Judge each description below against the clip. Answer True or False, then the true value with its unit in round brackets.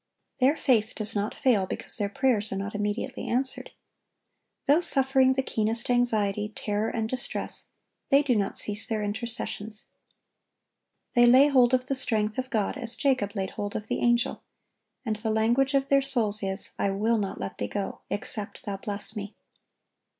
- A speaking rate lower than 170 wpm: False (175 wpm)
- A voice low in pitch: False (220 Hz)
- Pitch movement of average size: True (3.8 semitones)